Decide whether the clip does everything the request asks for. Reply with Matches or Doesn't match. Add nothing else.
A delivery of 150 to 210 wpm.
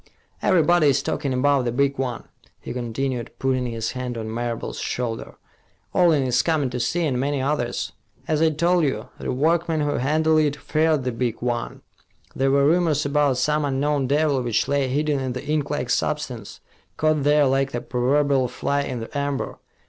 Matches